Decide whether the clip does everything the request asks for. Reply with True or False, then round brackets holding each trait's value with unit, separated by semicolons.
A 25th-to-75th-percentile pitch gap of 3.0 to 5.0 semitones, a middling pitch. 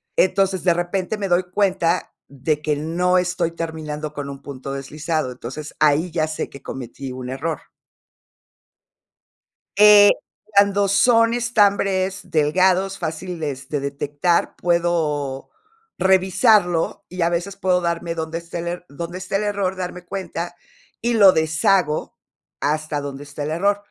True (3.9 semitones; 170 Hz)